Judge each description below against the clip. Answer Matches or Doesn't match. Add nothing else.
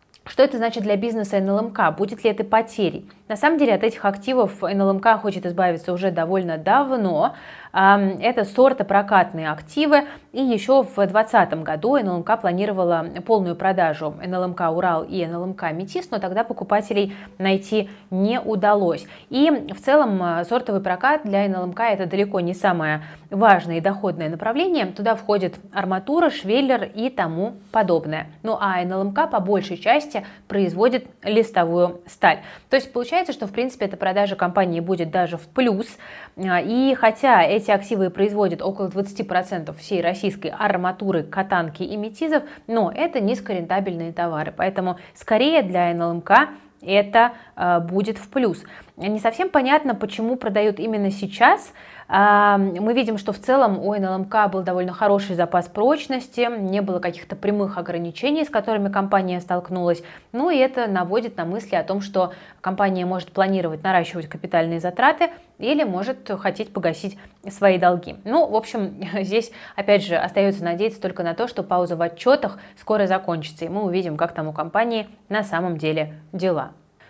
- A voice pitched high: Matches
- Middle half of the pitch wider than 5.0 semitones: Doesn't match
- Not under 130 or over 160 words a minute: Matches